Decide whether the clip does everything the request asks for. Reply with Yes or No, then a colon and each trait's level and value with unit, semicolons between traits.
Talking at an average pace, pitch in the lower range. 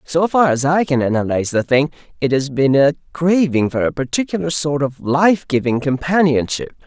No: average, 185 wpm; medium, 150 Hz